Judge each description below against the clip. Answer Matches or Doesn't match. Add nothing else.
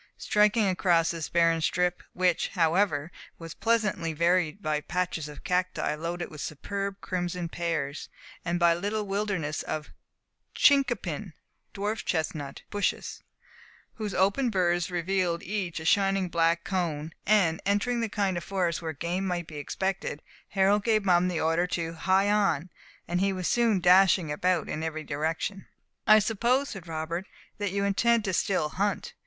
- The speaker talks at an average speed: Matches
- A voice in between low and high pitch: Matches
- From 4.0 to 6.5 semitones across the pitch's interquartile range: Doesn't match